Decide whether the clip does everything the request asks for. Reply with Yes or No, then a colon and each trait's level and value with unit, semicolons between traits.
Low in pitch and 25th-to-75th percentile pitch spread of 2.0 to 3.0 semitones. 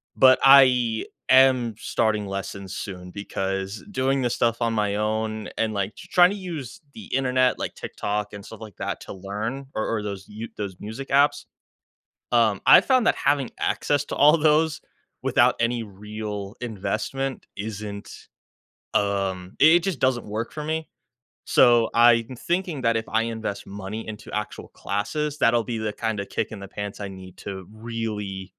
No: low, 110 Hz; average, 4.2 semitones